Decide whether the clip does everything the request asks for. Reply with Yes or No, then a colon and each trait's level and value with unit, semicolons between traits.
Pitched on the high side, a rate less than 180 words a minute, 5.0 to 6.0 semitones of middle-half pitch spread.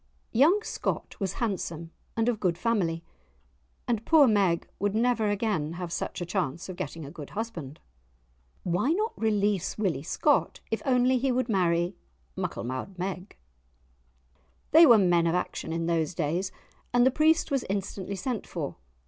Yes: high, 195 Hz; average, 155 wpm; wide, 5.6 semitones